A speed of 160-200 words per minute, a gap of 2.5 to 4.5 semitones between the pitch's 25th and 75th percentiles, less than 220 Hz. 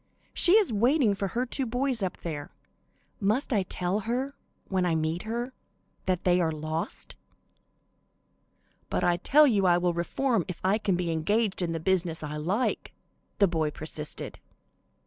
No: average, 165 wpm; wide, 5.6 semitones; high, 190 Hz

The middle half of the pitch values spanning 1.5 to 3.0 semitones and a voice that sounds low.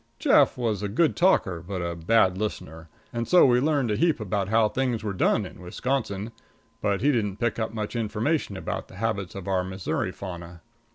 No: average, 4.0 semitones; low, 105 Hz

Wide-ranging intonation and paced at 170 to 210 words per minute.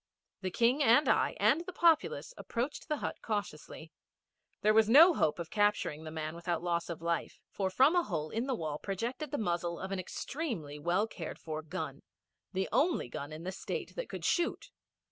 Yes: wide, 7.8 semitones; average, 195 wpm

